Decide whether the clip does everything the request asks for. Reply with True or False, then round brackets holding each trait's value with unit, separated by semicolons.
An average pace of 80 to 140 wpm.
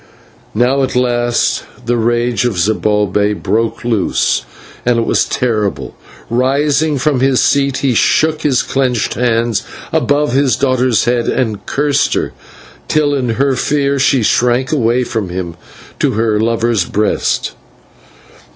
True (135 wpm)